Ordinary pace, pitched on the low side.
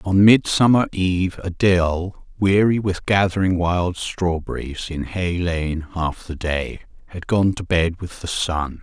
Yes: average, 150 wpm; very low, 90 Hz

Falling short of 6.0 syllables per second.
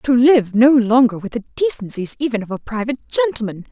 No: 6.3 syllables/s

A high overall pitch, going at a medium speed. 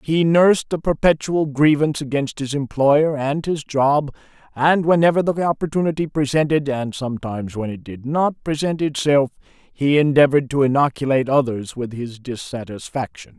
No: medium, 140 Hz; average, 145 wpm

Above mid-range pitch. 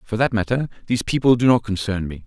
No: low, 110 Hz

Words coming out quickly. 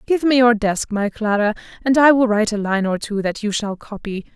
Yes: fast, 250 wpm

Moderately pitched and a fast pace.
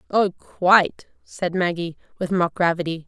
No: medium, 175 Hz; slow, 135 wpm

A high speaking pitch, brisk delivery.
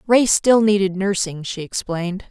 No: high, 195 Hz; average, 155 wpm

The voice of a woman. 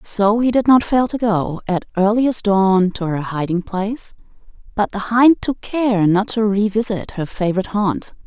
Yes: female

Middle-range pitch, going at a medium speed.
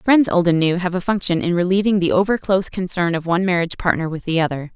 No: medium, 180 Hz; fast, 240 wpm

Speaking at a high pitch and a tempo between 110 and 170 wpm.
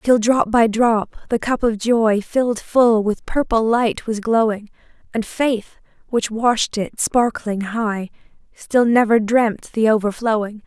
Yes: high, 225 Hz; average, 150 wpm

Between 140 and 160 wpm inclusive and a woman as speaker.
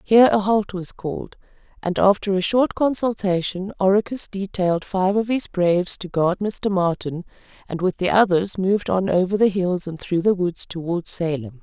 No: average, 180 wpm; female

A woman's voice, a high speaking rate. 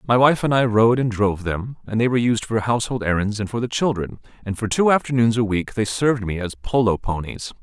No: male; fast, 245 wpm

